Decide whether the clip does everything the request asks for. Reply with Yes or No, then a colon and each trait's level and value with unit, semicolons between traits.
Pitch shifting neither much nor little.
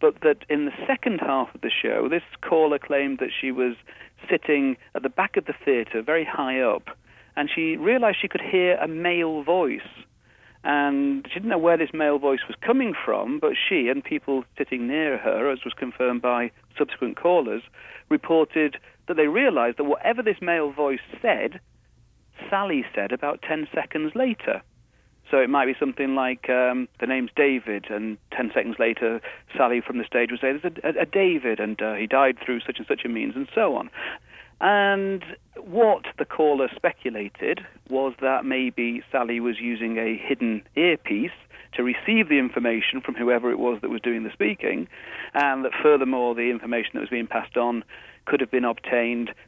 No: wide, 5.8 semitones